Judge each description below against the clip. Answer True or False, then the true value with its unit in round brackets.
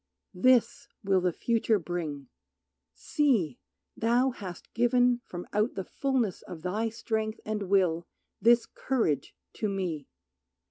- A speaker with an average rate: False (125 wpm)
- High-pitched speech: True (210 Hz)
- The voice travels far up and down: False (4.8 semitones)